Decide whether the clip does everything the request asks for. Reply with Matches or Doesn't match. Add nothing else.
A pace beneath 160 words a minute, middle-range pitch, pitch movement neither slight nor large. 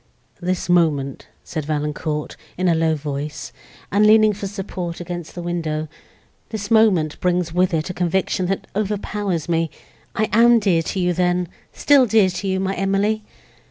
Matches